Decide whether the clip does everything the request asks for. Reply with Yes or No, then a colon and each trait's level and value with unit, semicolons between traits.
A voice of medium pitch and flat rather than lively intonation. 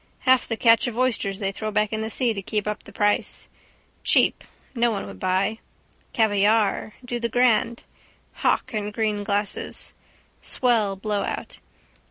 No: high, 215 Hz; narrow, 2.2 semitones